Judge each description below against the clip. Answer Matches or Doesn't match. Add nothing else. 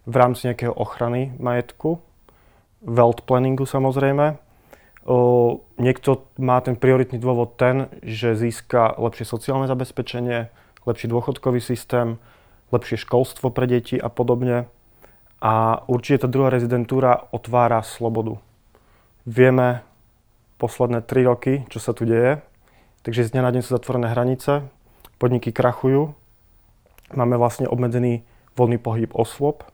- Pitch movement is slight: Matches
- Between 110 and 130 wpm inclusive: Matches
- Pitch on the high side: Doesn't match